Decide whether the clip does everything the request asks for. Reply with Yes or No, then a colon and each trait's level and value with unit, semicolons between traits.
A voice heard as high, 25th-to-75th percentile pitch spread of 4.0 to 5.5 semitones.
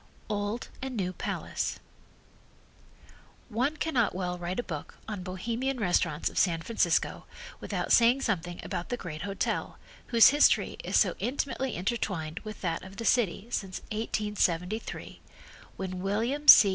Yes: high, 205 Hz; average, 4.8 semitones